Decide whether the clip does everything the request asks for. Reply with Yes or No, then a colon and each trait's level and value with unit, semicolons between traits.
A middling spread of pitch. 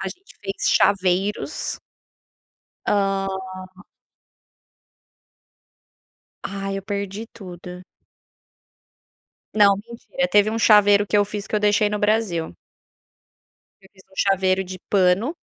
No: narrow, 1.5 semitones